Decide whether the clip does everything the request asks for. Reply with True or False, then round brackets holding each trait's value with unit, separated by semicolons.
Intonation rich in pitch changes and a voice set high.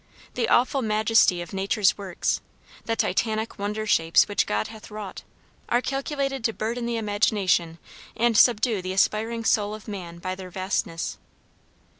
False (3.3 semitones; 215 Hz)